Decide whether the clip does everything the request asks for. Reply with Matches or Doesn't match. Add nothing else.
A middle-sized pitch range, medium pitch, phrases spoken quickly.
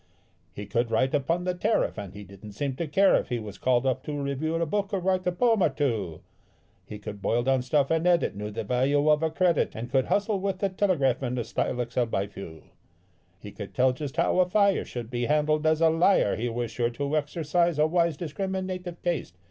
Doesn't match